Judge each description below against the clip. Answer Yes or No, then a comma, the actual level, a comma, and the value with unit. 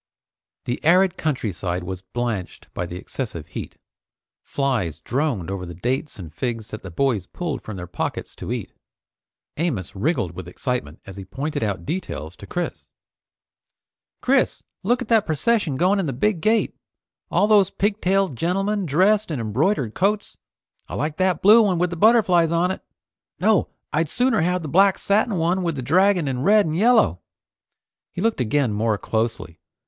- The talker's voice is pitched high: No, medium, 155 Hz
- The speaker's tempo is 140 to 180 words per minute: Yes, average, 165 wpm